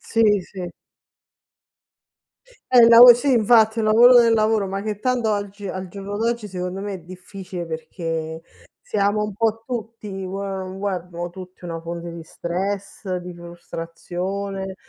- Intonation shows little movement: No, average, 3.4 semitones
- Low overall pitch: No, high, 195 Hz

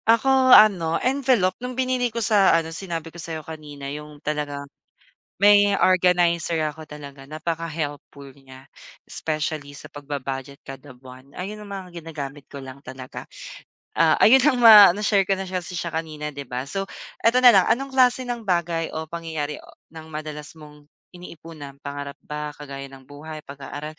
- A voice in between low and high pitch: Yes, medium, 160 Hz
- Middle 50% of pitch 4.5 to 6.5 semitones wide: Yes, average, 5.1 semitones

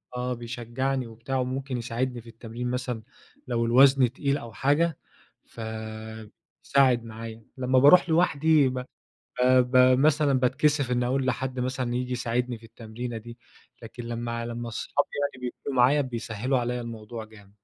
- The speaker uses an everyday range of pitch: No, narrow, 2.1 semitones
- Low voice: Yes, low, 125 Hz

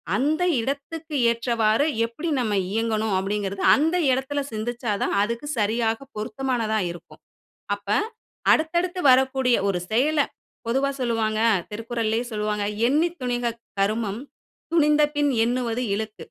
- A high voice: Yes, high, 235 Hz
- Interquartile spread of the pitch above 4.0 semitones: Yes, average, 4.5 semitones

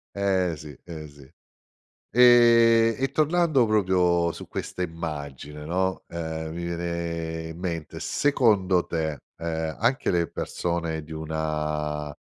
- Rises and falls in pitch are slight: No, average, 3.7 semitones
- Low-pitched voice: Yes, very low, 85 Hz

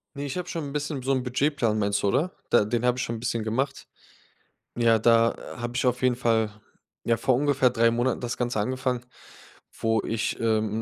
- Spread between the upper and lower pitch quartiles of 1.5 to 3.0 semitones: Yes, narrow, 2.4 semitones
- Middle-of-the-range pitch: No, low, 120 Hz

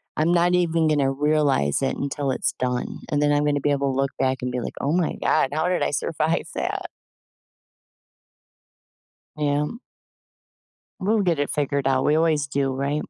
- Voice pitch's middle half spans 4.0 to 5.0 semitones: No, narrow, 2.5 semitones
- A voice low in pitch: No, medium, 145 Hz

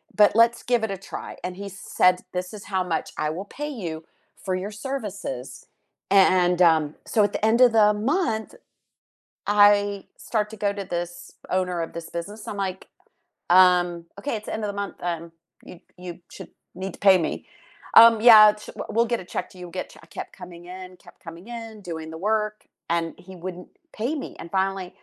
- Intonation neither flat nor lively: Yes, average, 3.2 semitones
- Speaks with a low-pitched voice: No, high, 195 Hz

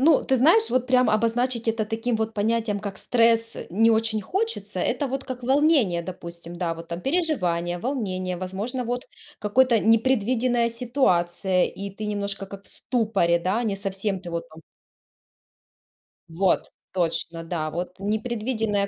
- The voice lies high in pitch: Yes, high, 215 Hz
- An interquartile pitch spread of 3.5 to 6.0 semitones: Yes, average, 4.9 semitones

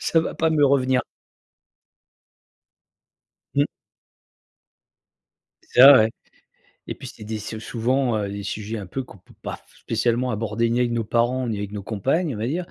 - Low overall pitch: Yes, low, 115 Hz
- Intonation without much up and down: No, average, 3.4 semitones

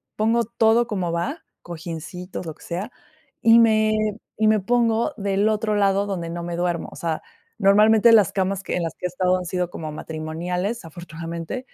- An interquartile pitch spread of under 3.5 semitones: No, average, 4.2 semitones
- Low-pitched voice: No, high, 190 Hz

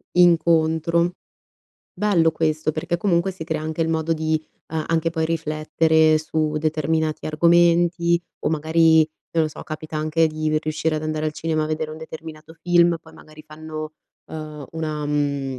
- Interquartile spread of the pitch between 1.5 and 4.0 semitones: No, narrow, 1.1 semitones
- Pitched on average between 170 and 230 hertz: No, medium, 160 Hz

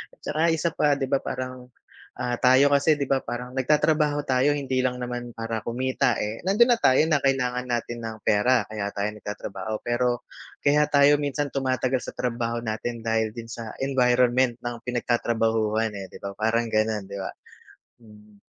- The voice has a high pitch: No, low, 125 Hz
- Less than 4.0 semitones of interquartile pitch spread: Yes, average, 3.1 semitones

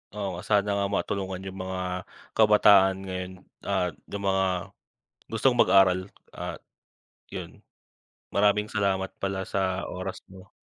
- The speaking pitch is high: No, very low, 95 Hz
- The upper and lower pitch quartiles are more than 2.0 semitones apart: No, narrow, 1.4 semitones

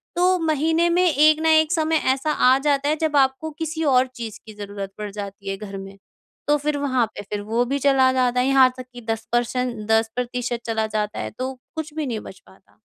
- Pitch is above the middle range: Yes, very high, 255 Hz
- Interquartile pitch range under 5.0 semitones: No, average, 5.3 semitones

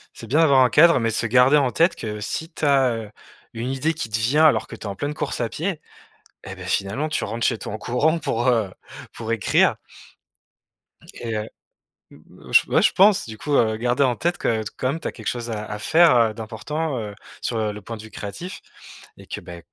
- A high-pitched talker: No, low, 120 Hz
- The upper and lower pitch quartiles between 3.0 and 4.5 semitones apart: No, average, 5.3 semitones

